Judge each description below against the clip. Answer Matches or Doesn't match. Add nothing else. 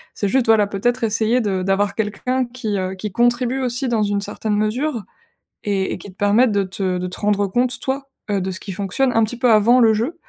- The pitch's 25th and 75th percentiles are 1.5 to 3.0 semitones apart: Doesn't match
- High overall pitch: Matches